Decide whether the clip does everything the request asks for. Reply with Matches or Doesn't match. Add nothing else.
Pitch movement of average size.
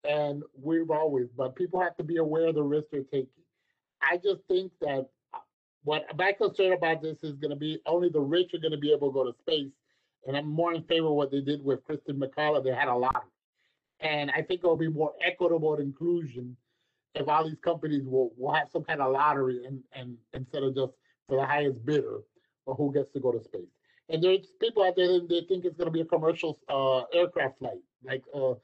Matches